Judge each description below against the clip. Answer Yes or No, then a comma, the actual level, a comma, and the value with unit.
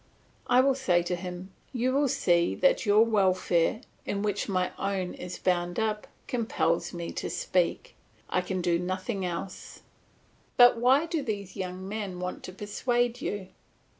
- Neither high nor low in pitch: No, high, 195 Hz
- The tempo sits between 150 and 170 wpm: Yes, average, 160 wpm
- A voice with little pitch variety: No, average, 4.3 semitones